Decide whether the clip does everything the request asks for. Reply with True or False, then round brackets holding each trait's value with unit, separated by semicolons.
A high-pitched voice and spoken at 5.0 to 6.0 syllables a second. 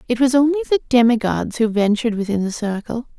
False (235 Hz; 6.3 syllables/s)